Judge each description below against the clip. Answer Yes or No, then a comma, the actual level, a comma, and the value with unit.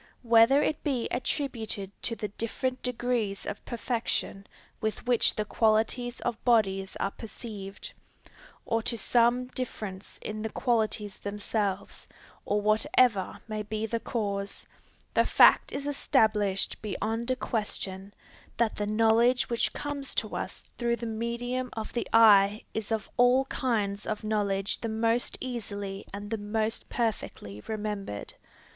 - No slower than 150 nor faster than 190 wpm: No, average, 140 wpm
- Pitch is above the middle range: Yes, high, 220 Hz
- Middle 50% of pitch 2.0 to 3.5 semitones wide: Yes, average, 2.7 semitones